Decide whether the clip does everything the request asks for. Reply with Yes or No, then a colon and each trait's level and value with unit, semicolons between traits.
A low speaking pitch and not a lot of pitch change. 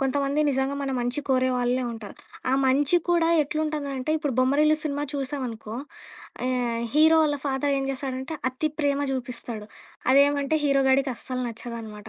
No: very high, 270 Hz; narrow, 2.3 semitones